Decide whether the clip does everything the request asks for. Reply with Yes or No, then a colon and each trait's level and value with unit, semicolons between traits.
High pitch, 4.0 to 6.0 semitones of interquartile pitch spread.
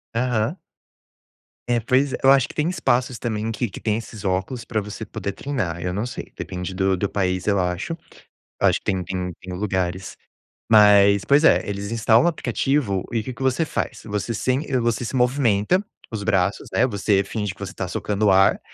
No: low, 105 Hz; average, 4.3 semitones